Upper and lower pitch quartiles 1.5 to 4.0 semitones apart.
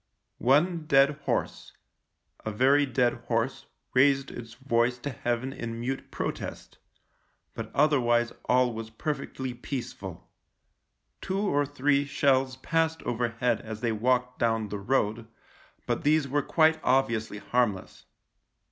Yes: average, 3.3 semitones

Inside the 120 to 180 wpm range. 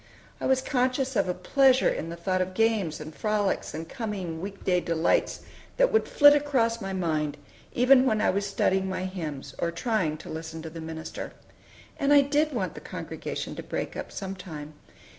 No: average, 195 wpm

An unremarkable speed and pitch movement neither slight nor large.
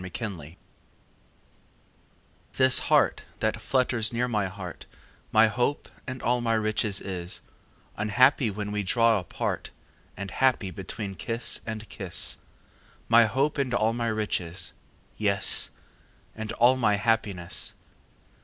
No: slow, 120 wpm; average, 3.3 semitones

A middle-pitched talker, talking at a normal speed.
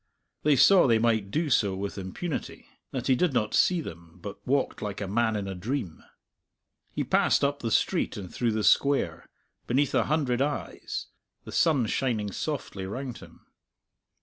No: low, 120 Hz; average, 175 wpm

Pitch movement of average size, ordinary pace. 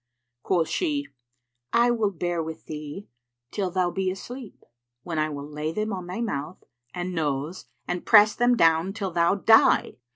Yes: average, 4.7 semitones; average, 165 wpm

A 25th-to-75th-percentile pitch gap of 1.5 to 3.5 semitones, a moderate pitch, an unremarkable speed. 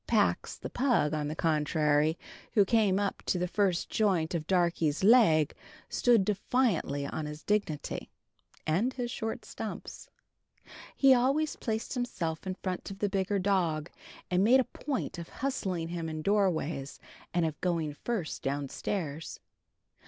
No: average, 5.3 semitones; medium, 180 Hz; average, 145 wpm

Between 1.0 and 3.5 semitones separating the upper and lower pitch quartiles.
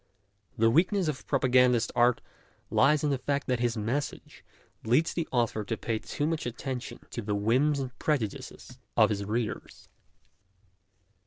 No: average, 4.1 semitones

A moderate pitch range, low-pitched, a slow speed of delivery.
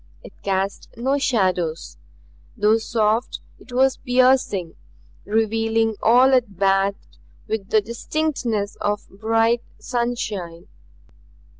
No: average, 3.5 semitones; high, 225 Hz; slow, 100 wpm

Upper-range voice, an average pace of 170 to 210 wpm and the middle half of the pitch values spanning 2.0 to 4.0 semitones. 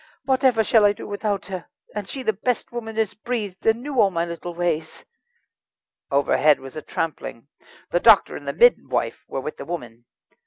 No: high, 200 Hz; average, 185 wpm; wide, 5.4 semitones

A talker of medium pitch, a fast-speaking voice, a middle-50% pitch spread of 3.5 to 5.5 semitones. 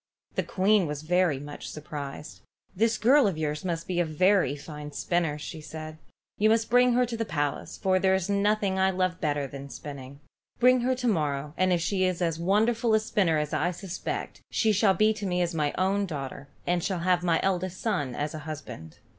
Yes: medium, 180 Hz; fast, 210 wpm; average, 5.1 semitones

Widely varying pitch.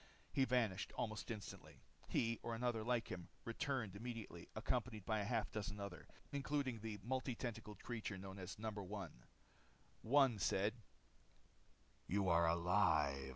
No: average, 3.7 semitones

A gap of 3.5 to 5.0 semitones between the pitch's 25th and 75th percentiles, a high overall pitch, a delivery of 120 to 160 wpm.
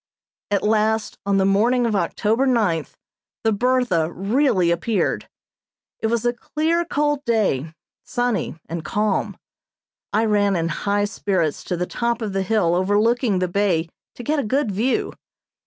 Yes: average, 4.2 semitones; high, 210 Hz; average, 155 wpm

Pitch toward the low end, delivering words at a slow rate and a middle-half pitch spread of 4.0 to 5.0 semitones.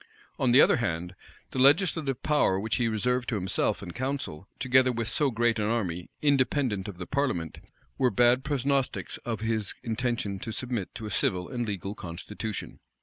No: low, 115 Hz; average, 175 wpm; average, 4.5 semitones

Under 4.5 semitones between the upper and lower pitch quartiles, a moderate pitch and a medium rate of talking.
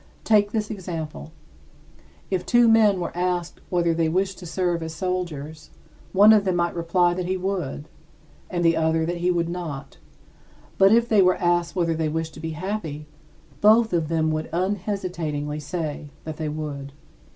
Yes: average, 3.0 semitones; medium, 175 Hz; average, 175 wpm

